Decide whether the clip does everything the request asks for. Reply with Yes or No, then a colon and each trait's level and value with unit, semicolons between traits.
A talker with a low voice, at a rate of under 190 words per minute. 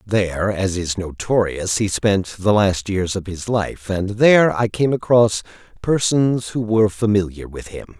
Yes: low, 100 Hz; average, 175 wpm